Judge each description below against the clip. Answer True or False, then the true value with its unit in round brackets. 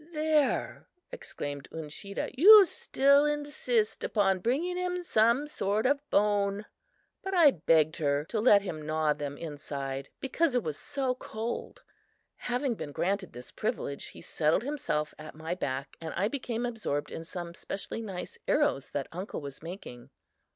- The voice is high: True (200 Hz)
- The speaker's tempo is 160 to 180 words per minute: False (150 wpm)